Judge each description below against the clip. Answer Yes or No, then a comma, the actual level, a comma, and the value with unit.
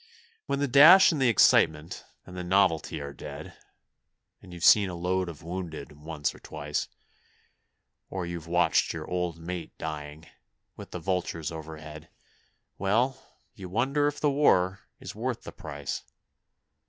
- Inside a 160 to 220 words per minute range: No, average, 150 wpm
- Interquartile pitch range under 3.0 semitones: No, average, 4.2 semitones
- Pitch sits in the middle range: No, very low, 90 Hz